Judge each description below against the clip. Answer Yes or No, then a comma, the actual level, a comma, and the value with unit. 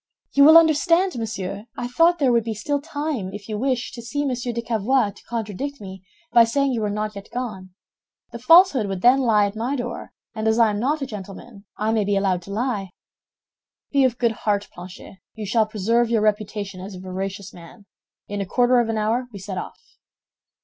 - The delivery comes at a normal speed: No, fast, 210 wpm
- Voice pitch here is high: Yes, high, 225 Hz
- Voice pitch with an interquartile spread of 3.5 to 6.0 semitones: Yes, average, 3.9 semitones